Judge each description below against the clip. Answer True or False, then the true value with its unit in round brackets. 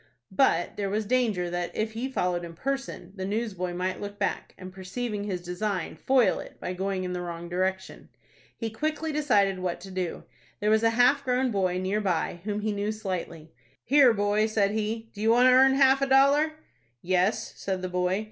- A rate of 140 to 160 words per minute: False (195 wpm)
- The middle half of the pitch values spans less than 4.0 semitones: False (4.4 semitones)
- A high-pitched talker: True (205 Hz)